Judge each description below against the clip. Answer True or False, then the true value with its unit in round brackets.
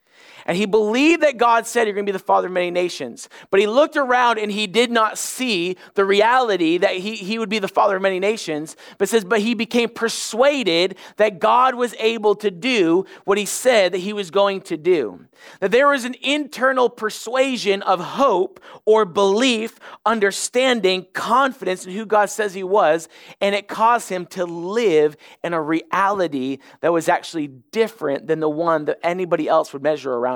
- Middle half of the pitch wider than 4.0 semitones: True (4.5 semitones)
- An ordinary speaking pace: True (190 wpm)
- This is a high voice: True (210 Hz)